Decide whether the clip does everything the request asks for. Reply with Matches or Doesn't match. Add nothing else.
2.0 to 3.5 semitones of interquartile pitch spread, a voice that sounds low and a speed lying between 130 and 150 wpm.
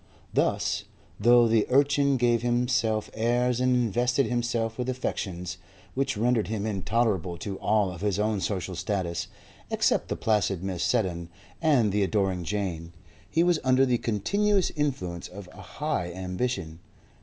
Doesn't match